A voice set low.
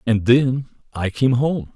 Yes: low, 120 Hz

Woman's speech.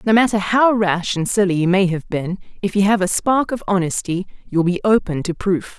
Yes: female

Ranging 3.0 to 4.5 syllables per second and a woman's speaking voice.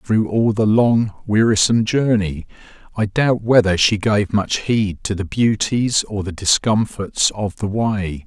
No: 4.0 syllables/s; male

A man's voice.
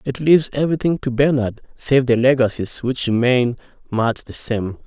Yes: male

